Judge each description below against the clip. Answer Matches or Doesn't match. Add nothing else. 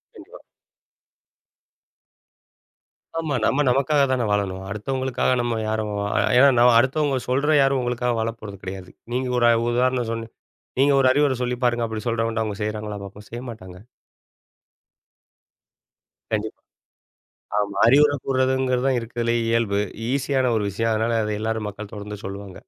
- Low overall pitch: Matches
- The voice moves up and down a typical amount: Matches